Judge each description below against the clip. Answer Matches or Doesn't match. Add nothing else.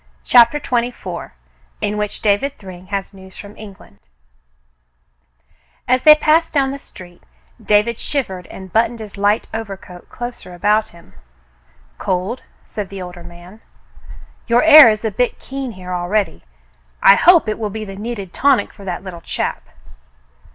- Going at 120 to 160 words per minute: Matches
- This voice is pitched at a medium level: Doesn't match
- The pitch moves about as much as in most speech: Matches